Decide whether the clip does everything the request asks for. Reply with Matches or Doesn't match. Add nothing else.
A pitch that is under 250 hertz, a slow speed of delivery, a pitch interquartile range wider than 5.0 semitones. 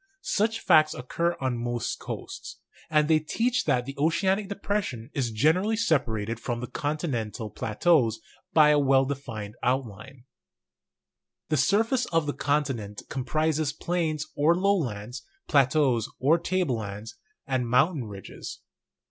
Matches